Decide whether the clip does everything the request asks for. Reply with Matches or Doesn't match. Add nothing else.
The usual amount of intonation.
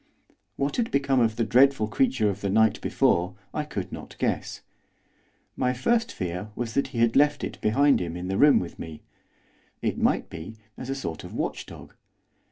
Doesn't match